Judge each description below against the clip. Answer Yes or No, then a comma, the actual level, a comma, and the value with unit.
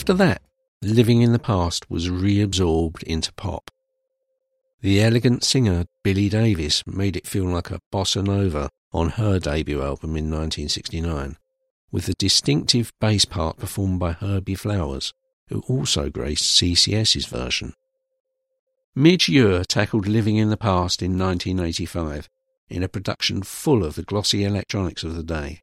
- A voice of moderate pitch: No, low, 100 Hz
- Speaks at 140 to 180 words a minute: Yes, average, 145 wpm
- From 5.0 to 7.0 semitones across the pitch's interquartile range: Yes, average, 5.3 semitones